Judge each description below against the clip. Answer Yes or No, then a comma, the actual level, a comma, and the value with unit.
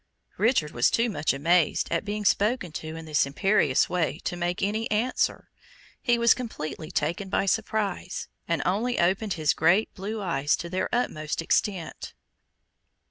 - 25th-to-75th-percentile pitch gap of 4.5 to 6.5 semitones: Yes, average, 5.0 semitones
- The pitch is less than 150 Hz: No, medium, 185 Hz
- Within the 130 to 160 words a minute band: Yes, average, 155 wpm